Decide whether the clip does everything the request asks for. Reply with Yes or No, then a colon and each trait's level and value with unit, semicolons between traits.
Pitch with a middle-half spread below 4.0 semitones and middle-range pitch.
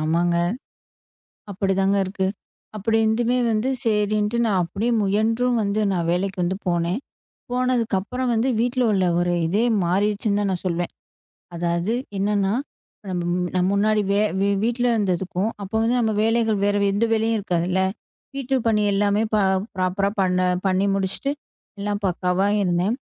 No: average, 3.3 semitones; high, 200 Hz